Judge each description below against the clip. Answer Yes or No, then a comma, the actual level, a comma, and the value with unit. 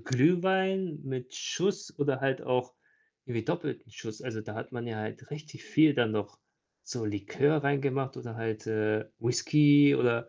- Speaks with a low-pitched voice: Yes, low, 130 Hz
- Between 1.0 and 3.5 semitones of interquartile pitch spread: No, average, 4.5 semitones